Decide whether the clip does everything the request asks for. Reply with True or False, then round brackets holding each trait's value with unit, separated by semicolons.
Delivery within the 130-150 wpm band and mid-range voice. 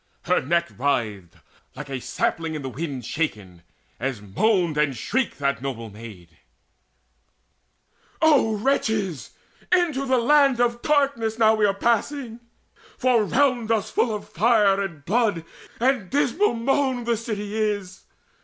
False (140 wpm; 210 Hz)